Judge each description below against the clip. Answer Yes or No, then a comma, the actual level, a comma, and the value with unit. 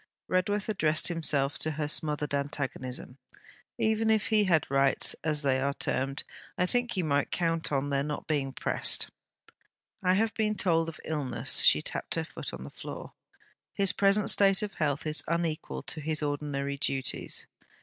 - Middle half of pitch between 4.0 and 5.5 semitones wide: Yes, average, 4.7 semitones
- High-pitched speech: No, medium, 155 Hz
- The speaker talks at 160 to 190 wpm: Yes, average, 170 wpm